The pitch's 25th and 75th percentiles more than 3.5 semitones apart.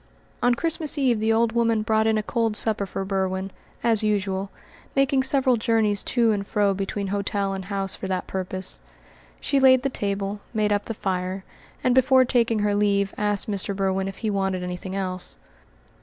No: average, 3.0 semitones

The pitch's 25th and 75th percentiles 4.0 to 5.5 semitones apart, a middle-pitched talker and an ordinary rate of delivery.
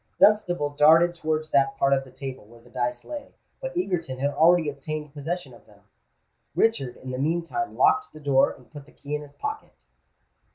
Yes: average, 4.4 semitones; medium, 150 Hz; average, 195 wpm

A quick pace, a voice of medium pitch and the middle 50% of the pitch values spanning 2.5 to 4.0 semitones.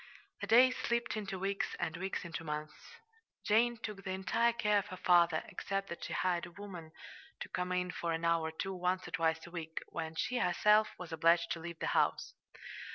Yes: fast, 215 wpm; medium, 180 Hz; average, 3.5 semitones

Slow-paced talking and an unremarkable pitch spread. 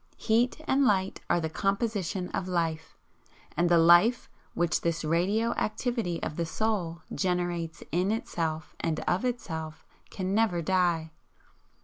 Yes: slow, 130 wpm; average, 4.3 semitones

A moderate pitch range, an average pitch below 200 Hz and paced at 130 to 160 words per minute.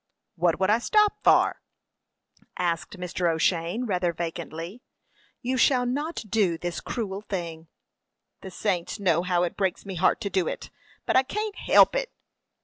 No: wide, 5.7 semitones; high, 190 Hz; average, 155 wpm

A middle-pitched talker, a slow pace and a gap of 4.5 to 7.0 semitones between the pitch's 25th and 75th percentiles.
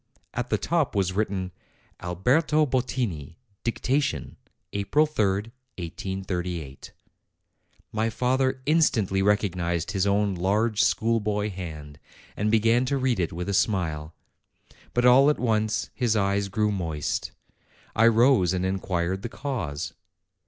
No: low, 105 Hz; slow, 125 wpm; average, 4.9 semitones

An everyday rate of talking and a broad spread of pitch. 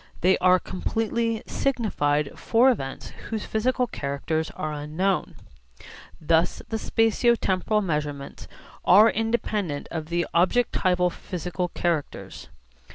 No: slow, 105 wpm; wide, 5.9 semitones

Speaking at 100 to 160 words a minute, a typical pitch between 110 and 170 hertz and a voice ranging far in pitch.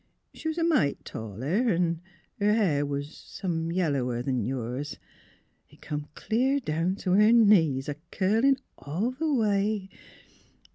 No: average, 145 wpm; medium, 180 Hz; wide, 7.2 semitones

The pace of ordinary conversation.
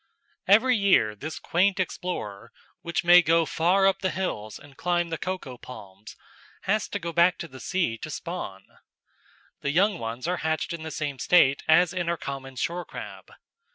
Yes: average, 180 wpm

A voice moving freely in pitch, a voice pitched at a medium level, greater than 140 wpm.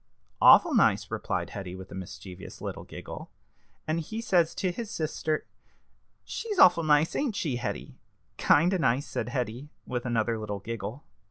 Yes: wide, 7.4 semitones; medium, 145 Hz; average, 160 wpm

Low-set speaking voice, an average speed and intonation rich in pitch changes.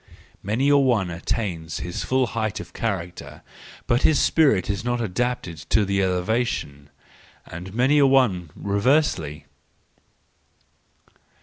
No: low, 105 Hz; slow, 115 wpm; wide, 5.7 semitones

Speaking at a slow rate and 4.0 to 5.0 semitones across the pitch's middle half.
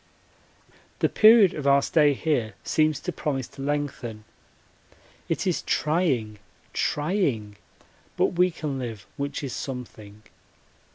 Yes: slow, 120 wpm; average, 4.7 semitones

